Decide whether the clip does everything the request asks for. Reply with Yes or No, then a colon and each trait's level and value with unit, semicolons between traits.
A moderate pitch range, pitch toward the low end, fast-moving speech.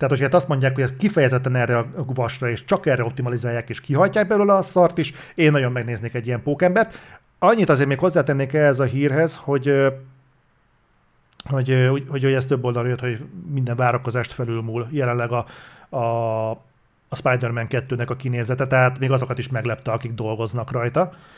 Yes: average, 3.0 semitones; low, 130 Hz; fast, 175 wpm